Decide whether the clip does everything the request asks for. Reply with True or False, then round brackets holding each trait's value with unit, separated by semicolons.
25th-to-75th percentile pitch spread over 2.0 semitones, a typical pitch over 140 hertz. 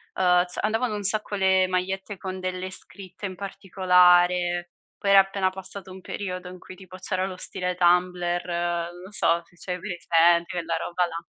False (1.4 semitones; 185 Hz)